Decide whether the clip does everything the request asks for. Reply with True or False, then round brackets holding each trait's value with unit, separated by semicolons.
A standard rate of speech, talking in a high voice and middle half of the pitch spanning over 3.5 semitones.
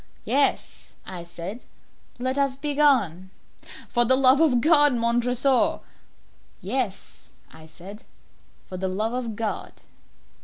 False (120 wpm; 240 Hz; 5.6 semitones)